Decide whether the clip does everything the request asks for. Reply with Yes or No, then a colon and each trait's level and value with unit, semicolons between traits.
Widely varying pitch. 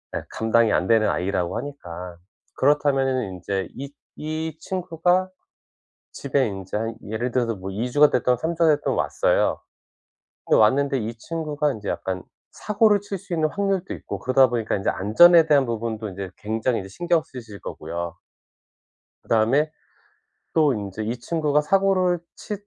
Yes: wide, 6.8 semitones